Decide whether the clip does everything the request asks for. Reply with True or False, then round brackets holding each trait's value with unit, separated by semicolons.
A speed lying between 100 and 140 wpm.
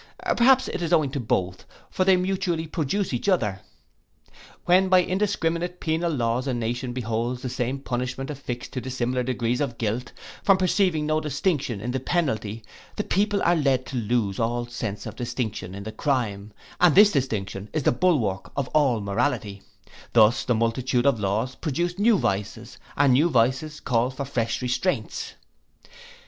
False (165 wpm)